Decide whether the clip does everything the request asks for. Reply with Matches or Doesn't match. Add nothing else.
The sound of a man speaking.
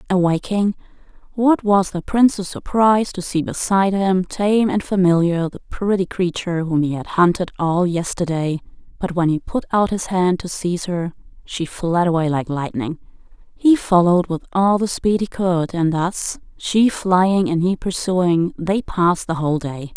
Doesn't match